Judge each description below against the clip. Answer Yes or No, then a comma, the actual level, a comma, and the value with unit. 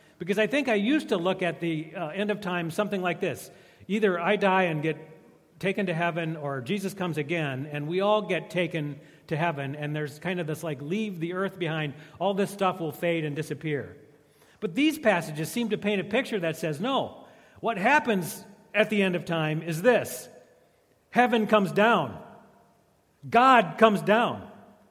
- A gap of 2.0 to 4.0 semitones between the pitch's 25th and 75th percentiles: No, average, 4.9 semitones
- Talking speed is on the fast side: No, average, 190 wpm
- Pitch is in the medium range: Yes, medium, 180 Hz